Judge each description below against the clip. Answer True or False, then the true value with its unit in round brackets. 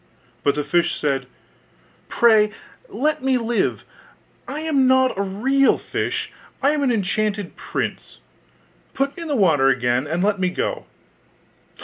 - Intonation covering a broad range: True (7.6 semitones)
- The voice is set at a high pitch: True (215 Hz)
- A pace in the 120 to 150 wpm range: True (145 wpm)